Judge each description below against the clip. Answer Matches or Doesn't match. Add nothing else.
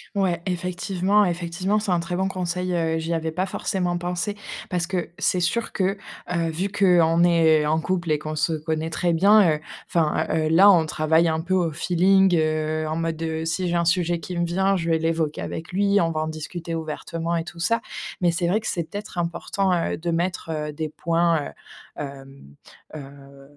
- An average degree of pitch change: Doesn't match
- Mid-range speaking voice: Matches